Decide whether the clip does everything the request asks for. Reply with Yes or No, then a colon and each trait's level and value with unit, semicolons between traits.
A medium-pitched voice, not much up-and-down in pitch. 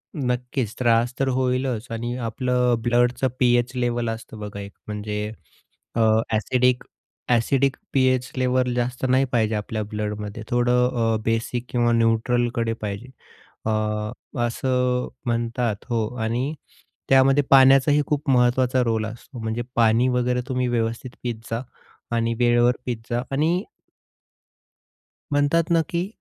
No: low, 120 Hz; narrow, 2.0 semitones